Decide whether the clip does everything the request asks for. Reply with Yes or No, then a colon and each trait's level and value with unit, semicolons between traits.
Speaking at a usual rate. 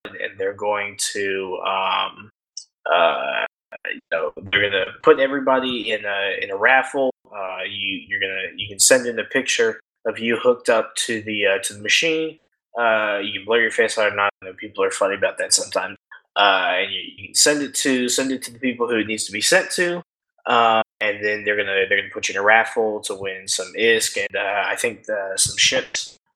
No: fast, 220 wpm